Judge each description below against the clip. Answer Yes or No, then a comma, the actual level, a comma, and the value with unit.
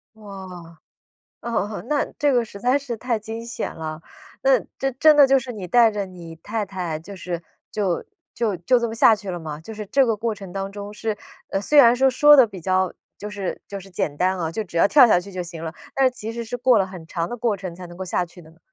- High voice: Yes, high, 205 Hz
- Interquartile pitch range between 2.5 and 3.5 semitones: No, average, 4.8 semitones